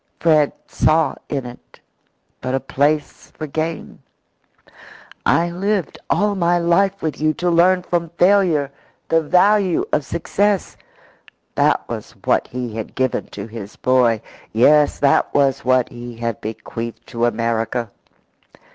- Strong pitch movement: Yes, wide, 6.1 semitones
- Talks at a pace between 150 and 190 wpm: No, slow, 135 wpm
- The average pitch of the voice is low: No, medium, 150 Hz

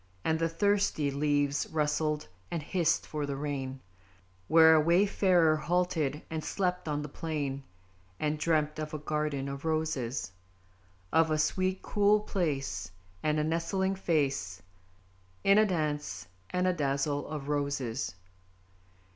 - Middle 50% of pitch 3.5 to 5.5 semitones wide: No, average, 2.8 semitones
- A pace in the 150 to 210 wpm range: No, slow, 135 wpm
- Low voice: No, medium, 155 Hz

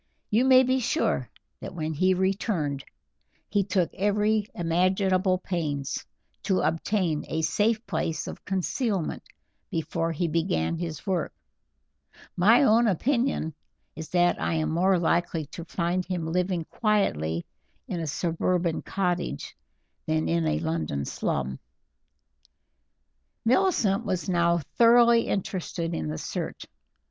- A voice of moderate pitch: Yes, medium, 175 Hz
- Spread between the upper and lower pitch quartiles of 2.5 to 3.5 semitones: No, average, 4.2 semitones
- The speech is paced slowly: Yes, slow, 125 wpm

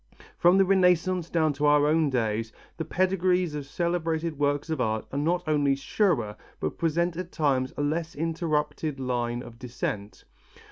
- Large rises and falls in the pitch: No, average, 4.1 semitones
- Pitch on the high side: No, medium, 150 Hz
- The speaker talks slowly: No, average, 160 wpm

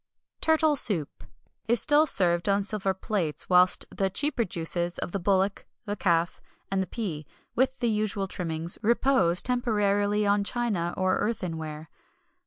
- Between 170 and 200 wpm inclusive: No, average, 145 wpm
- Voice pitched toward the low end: No, high, 195 Hz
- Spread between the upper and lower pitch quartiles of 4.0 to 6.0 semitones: Yes, average, 4.5 semitones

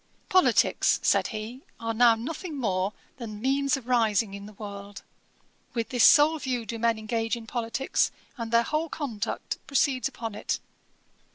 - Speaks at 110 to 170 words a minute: Yes, average, 160 wpm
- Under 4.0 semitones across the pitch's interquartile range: Yes, average, 3.5 semitones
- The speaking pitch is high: Yes, high, 230 Hz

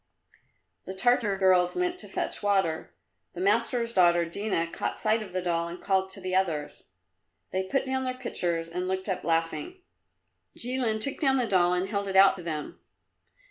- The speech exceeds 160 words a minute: Yes, average, 180 wpm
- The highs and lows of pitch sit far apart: No, average, 4.7 semitones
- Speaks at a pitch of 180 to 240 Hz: Yes, high, 190 Hz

